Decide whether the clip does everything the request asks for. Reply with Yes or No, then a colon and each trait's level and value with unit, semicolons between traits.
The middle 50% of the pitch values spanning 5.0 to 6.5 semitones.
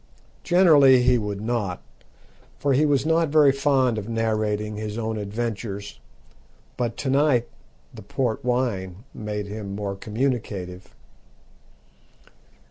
No: average, 4.2 semitones